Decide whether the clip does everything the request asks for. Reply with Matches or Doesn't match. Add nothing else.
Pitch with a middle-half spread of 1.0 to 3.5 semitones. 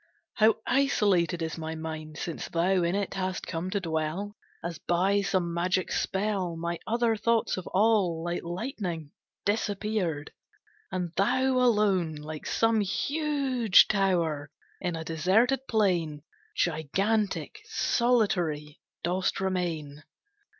Doesn't match